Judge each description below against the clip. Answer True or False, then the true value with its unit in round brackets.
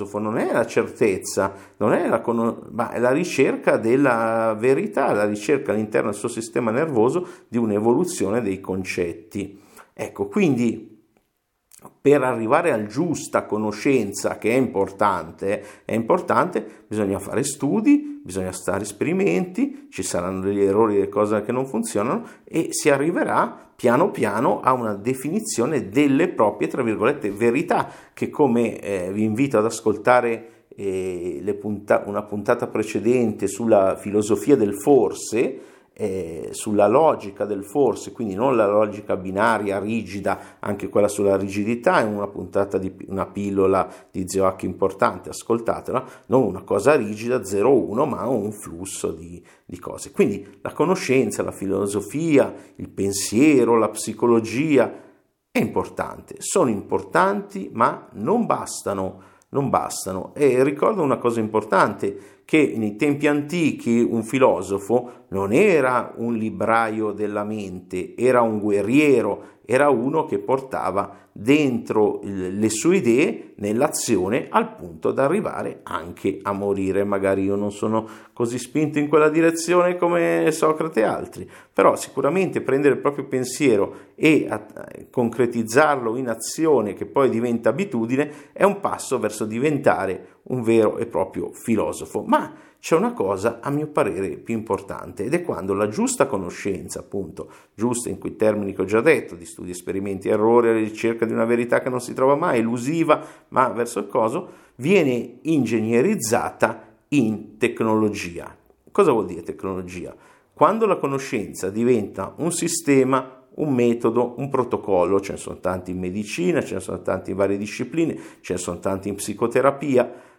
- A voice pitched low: True (115 Hz)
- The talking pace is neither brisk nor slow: True (145 wpm)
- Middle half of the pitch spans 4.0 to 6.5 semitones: True (4.3 semitones)